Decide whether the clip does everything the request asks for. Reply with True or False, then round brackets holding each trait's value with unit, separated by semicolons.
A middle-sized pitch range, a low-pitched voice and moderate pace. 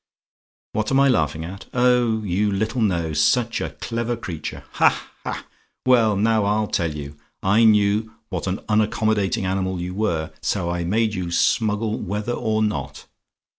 True (3.7 semitones; 105 Hz; 160 wpm)